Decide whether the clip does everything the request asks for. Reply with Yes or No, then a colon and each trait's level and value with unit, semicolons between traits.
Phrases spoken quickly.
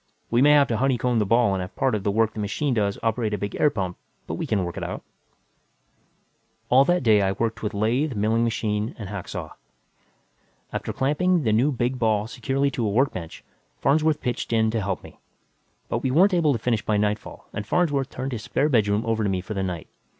Yes: fast, 225 wpm